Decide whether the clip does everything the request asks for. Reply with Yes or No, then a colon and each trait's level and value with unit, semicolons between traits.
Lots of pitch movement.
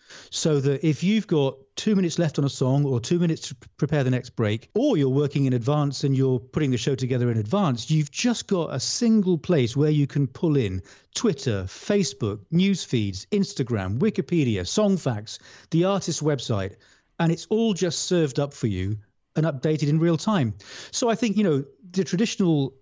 Yes: wide, 5.7 semitones